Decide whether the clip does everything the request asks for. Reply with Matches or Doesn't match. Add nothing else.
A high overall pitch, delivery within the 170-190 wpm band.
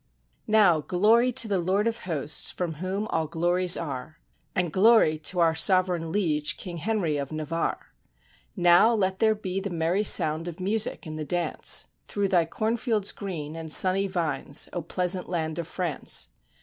Doesn't match